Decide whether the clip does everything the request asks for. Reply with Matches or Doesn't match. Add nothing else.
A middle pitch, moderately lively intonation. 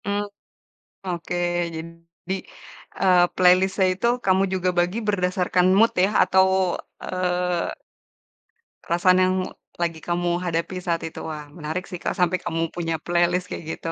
Doesn't match